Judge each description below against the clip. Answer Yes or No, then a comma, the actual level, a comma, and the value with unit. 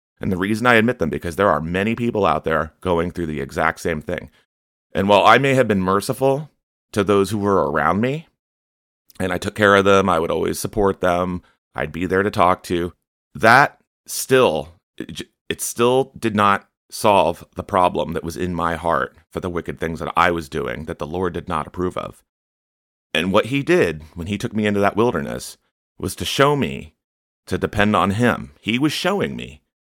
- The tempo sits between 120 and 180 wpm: No, fast, 205 wpm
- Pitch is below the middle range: Yes, very low, 95 Hz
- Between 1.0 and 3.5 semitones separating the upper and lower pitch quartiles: No, average, 4.1 semitones